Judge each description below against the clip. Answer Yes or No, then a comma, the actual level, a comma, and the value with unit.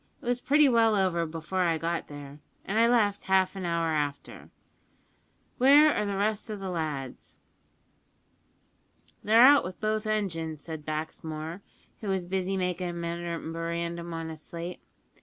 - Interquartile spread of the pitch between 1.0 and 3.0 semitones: No, average, 4.2 semitones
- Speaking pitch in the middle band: Yes, medium, 175 Hz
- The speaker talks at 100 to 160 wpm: Yes, average, 155 wpm